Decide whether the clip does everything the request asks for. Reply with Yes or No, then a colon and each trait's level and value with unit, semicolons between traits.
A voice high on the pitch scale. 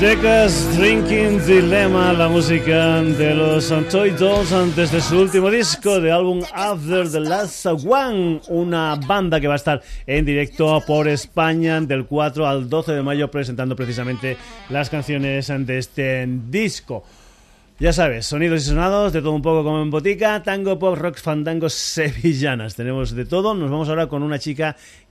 No: medium, 160 Hz